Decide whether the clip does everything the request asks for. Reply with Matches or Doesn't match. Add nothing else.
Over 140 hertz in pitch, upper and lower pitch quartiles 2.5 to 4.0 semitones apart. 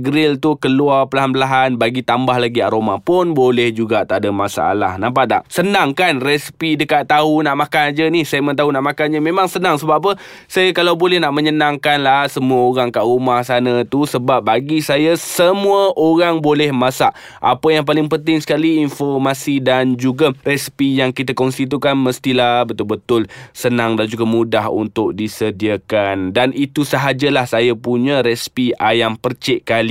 Doesn't match